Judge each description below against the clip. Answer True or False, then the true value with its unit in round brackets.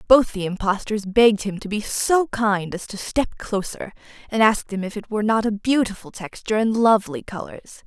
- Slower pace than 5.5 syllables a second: True (5.3 syllables/s)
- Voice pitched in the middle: False (210 Hz)